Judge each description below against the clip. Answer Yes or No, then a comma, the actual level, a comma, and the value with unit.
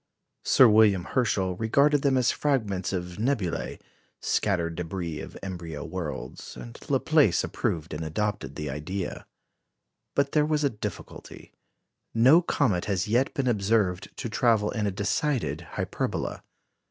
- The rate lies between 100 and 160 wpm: Yes, average, 140 wpm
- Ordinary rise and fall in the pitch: No, wide, 5.9 semitones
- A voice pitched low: Yes, low, 100 Hz